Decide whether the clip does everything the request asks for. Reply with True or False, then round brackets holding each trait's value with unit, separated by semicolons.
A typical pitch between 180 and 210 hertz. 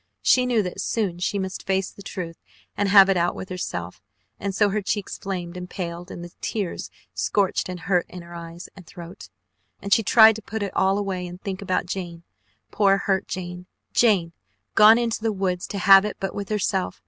True (190 Hz)